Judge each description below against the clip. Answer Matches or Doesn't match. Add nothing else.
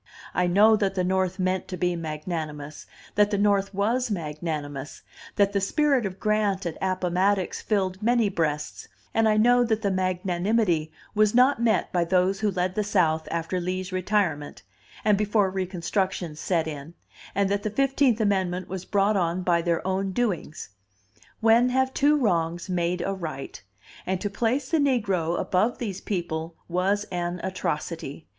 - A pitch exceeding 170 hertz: Matches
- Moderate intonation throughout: Matches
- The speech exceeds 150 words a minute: Matches